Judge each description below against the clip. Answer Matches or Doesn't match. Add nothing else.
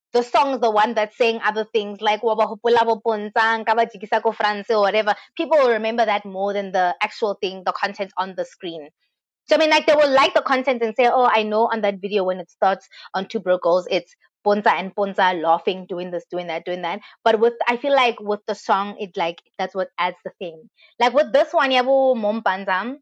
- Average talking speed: Doesn't match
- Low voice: Doesn't match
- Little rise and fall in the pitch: Doesn't match